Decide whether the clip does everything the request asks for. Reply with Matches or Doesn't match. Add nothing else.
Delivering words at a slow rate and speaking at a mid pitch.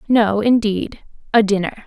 Doesn't match